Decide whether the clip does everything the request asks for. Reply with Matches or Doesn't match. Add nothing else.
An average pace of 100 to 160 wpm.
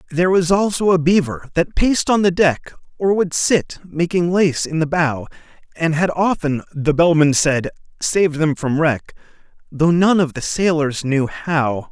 Doesn't match